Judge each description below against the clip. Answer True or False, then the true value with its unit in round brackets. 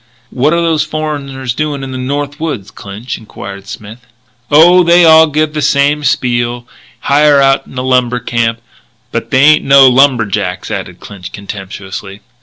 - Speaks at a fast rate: False (160 wpm)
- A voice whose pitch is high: False (135 Hz)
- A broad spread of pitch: False (4.6 semitones)